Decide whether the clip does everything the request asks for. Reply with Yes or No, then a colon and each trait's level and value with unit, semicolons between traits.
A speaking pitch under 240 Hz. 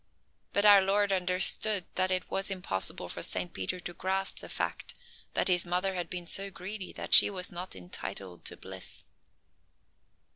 Yes: medium, 185 Hz